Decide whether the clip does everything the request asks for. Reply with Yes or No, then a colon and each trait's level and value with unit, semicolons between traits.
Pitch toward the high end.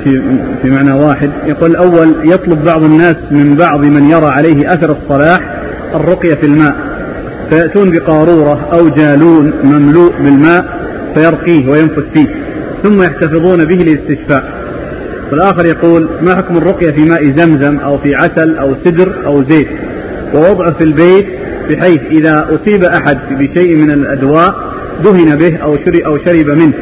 No: medium, 160 Hz